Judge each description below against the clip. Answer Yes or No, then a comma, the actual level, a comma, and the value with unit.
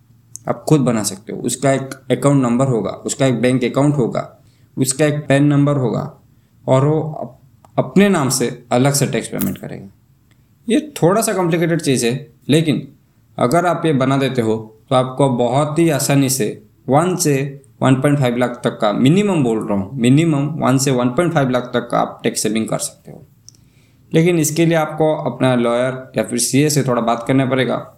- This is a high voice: No, low, 130 Hz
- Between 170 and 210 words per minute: Yes, average, 185 wpm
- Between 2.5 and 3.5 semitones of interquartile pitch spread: Yes, average, 3.2 semitones